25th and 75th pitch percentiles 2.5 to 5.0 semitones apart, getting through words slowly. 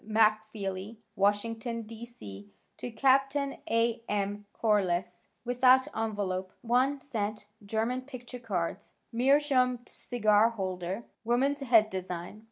Yes: average, 3.5 semitones; slow, 105 wpm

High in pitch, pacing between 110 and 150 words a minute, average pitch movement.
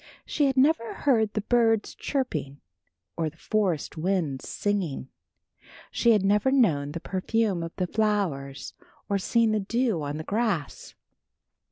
No: high, 200 Hz; average, 145 wpm; wide, 6.0 semitones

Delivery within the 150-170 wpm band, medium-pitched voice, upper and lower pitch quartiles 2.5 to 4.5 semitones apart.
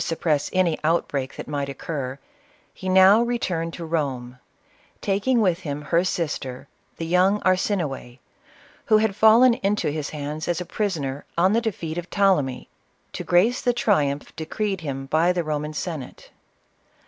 No: average, 155 wpm; medium, 165 Hz; average, 5.0 semitones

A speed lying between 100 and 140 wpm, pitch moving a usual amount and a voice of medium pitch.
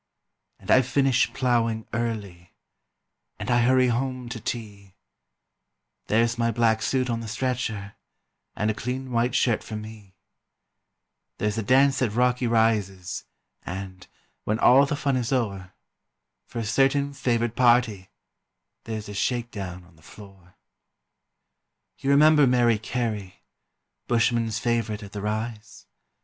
No: slow, 135 wpm; average, 3.0 semitones; low, 115 Hz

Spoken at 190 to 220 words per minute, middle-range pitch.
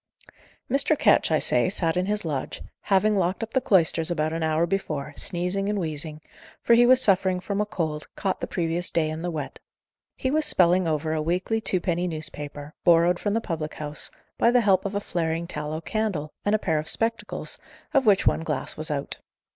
Yes: average, 200 wpm; medium, 175 Hz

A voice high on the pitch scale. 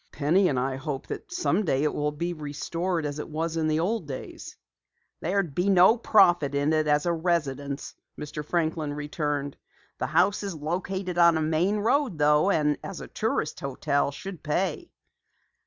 No: medium, 160 Hz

